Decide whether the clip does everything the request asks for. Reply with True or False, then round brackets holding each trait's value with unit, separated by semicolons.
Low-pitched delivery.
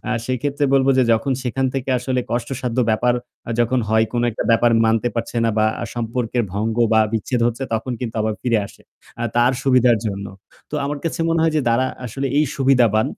True (120 Hz)